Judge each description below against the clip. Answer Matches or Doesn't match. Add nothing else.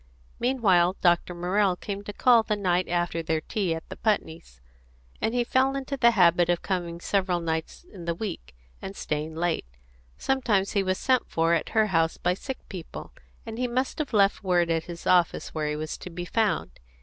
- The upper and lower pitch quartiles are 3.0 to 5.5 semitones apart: Matches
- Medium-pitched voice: Matches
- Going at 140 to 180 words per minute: Doesn't match